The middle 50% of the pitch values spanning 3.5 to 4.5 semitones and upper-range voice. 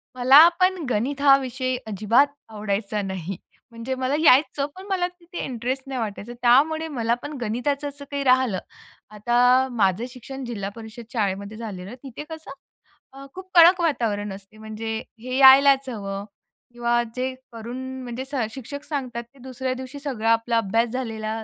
Yes: average, 3.8 semitones; very high, 250 Hz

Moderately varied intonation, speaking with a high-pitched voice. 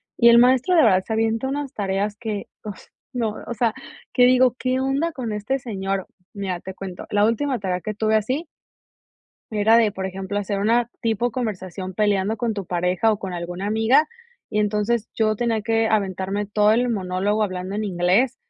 Yes: average, 3.3 semitones; high, 215 Hz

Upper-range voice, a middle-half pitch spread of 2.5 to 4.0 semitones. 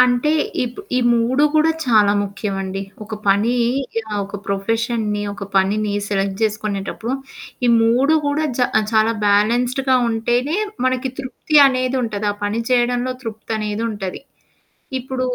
Yes: high, 225 Hz; average, 3.6 semitones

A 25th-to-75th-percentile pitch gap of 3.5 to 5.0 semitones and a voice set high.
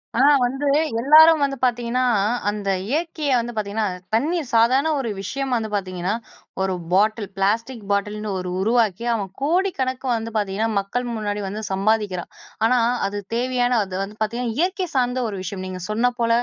Yes: average, 4.0 semitones; high, 230 Hz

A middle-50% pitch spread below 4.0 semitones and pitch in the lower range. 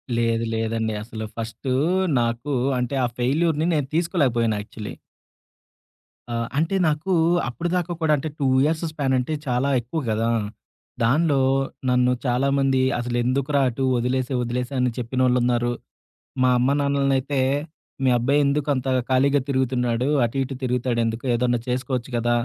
Yes: average, 2.8 semitones; low, 130 Hz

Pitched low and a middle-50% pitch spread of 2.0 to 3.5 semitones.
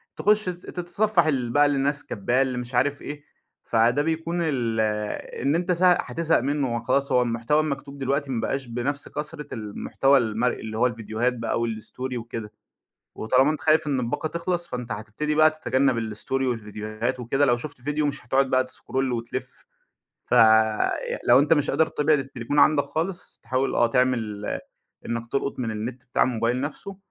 No: low, 130 Hz; average, 4.0 semitones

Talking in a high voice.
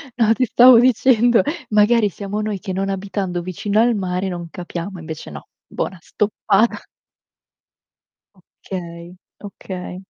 Yes: high, 195 Hz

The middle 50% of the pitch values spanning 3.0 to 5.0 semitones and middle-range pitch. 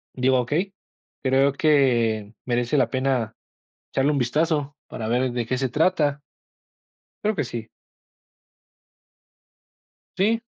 No: average, 3.6 semitones; low, 130 Hz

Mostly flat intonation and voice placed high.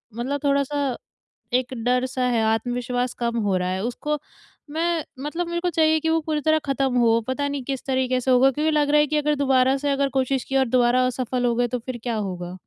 No: average, 3.1 semitones; very high, 260 Hz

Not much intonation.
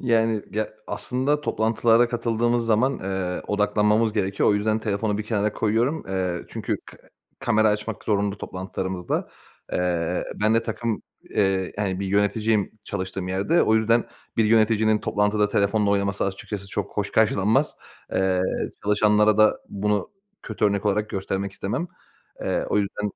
Yes: narrow, 2.0 semitones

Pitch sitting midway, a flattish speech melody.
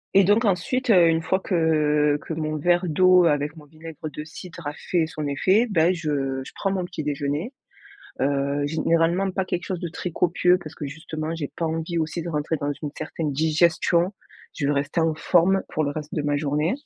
No: medium, 160 Hz; average, 3.0 semitones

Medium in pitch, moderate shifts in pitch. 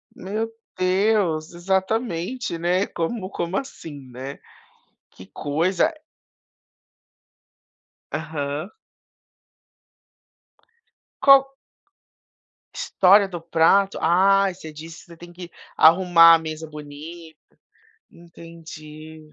Yes: medium, 170 Hz; average, 3.3 semitones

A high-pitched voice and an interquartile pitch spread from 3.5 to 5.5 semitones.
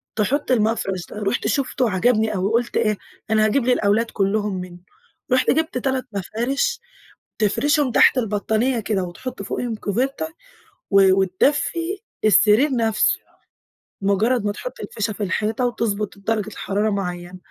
Yes: high, 215 Hz; average, 3.9 semitones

